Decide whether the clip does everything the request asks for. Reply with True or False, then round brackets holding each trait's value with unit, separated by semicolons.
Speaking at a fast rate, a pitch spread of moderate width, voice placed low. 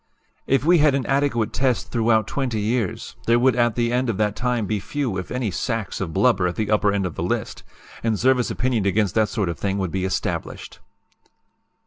True (210 wpm; 3.9 semitones; 115 Hz)